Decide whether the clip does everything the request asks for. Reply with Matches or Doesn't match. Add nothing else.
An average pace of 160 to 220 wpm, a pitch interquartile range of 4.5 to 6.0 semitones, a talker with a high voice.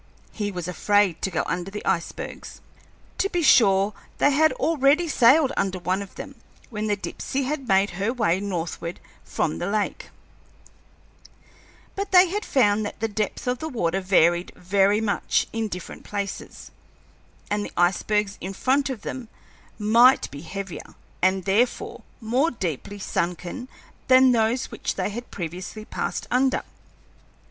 Doesn't match